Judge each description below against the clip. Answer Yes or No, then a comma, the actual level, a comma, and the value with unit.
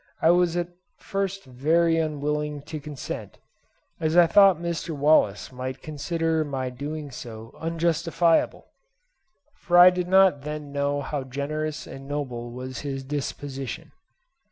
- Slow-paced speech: Yes, slow, 130 wpm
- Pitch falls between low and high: Yes, medium, 150 Hz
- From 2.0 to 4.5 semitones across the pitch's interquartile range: Yes, average, 3.4 semitones